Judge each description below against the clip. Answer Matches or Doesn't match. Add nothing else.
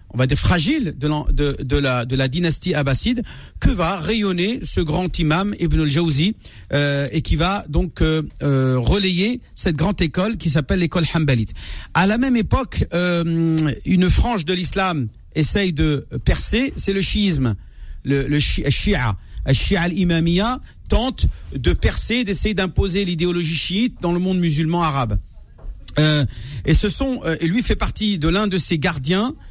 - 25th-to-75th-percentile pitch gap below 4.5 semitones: Doesn't match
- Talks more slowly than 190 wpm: Matches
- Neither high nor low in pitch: Matches